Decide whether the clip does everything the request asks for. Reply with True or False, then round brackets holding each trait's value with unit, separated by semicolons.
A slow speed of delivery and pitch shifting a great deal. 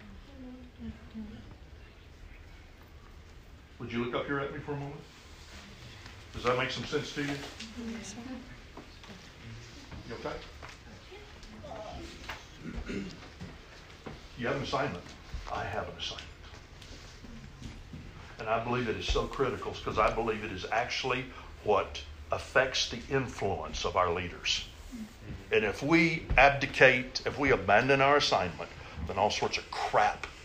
True (120 wpm; 8.4 semitones)